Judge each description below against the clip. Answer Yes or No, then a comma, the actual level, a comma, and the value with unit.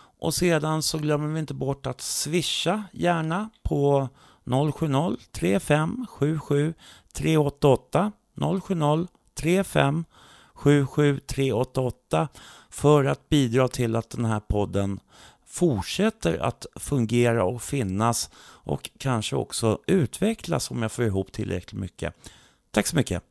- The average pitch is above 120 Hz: Yes, medium, 140 Hz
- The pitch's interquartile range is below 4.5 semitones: No, average, 5.0 semitones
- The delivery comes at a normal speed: No, slow, 115 wpm